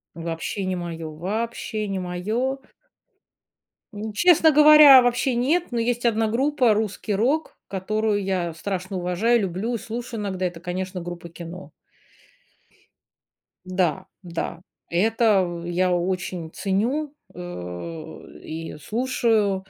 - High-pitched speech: Yes, high, 195 Hz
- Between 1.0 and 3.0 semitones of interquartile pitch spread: No, average, 4.8 semitones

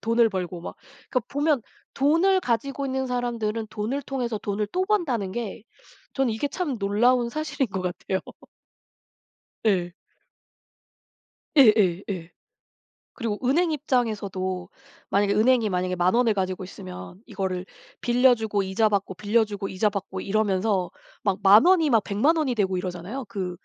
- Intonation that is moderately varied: Yes, average, 4.9 semitones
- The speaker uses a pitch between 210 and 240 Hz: Yes, high, 215 Hz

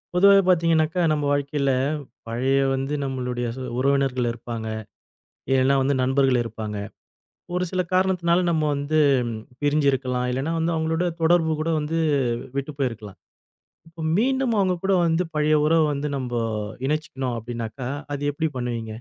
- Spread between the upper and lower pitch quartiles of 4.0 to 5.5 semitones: Yes, average, 4.3 semitones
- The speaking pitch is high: No, medium, 140 Hz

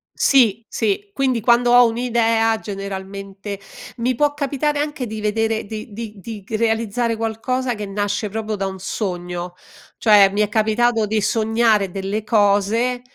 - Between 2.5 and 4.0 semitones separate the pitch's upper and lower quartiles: Yes, average, 2.8 semitones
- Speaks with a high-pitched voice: Yes, high, 220 Hz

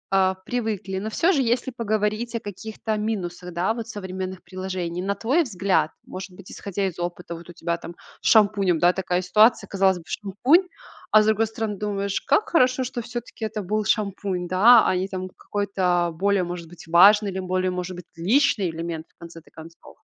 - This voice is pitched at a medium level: No, high, 195 Hz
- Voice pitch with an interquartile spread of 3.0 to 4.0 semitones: Yes, average, 3.4 semitones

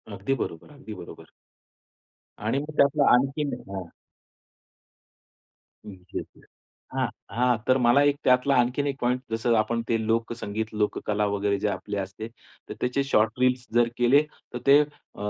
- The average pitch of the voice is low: Yes, low, 120 Hz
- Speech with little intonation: No, average, 4.0 semitones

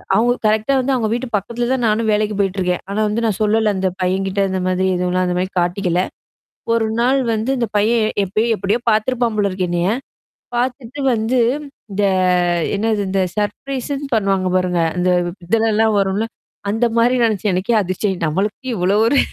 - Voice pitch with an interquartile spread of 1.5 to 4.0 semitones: Yes, average, 3.5 semitones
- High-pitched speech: Yes, high, 210 Hz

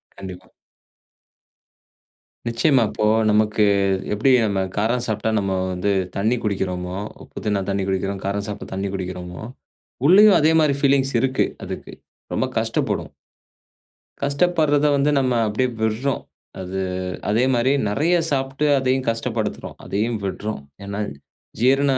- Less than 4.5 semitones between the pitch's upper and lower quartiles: No, average, 5.3 semitones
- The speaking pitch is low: Yes, low, 110 Hz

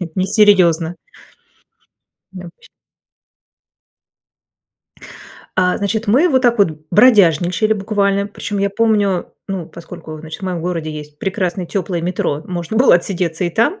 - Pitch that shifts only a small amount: No, average, 3.3 semitones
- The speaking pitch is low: No, medium, 185 Hz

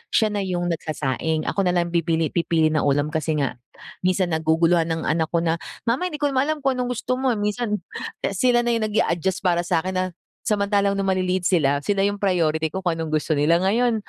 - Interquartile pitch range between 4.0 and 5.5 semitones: Yes, average, 4.4 semitones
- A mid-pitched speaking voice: Yes, medium, 180 Hz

